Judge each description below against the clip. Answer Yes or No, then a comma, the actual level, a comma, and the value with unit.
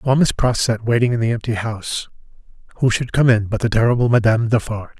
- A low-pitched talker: Yes, low, 115 Hz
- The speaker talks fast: Yes, fast, 215 wpm